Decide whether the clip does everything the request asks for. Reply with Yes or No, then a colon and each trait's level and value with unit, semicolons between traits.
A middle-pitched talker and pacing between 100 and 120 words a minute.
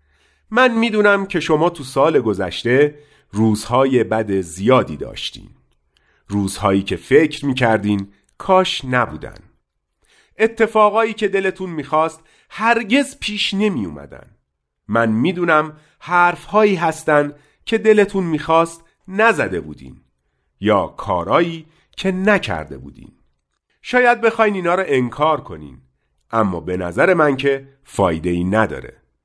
Yes: medium, 145 Hz; average, 110 wpm